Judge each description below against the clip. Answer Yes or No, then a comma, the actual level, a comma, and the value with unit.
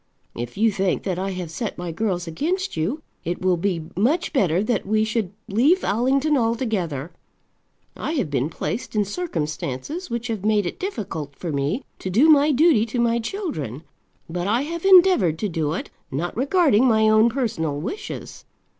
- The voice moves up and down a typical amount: No, wide, 7.5 semitones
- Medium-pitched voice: No, high, 215 Hz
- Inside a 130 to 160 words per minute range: No, average, 175 wpm